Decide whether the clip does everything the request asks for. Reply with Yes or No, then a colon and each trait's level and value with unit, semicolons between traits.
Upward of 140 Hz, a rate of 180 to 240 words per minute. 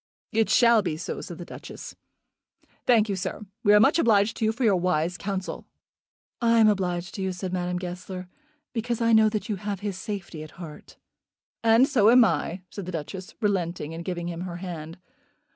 Yes: high, 190 Hz; average, 195 wpm